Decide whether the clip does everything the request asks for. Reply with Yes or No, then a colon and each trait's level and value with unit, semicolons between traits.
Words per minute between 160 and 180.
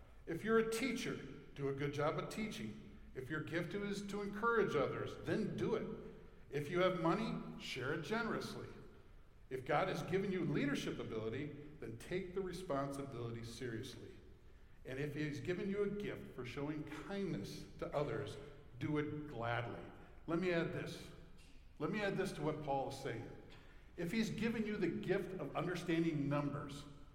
Yes: average, 170 wpm